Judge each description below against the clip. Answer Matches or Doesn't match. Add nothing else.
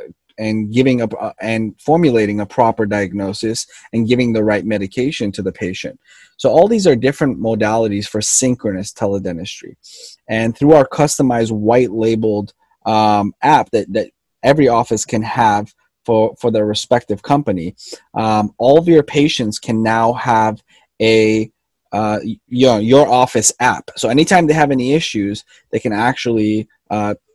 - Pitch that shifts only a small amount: Doesn't match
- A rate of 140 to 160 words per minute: Matches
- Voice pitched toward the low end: Matches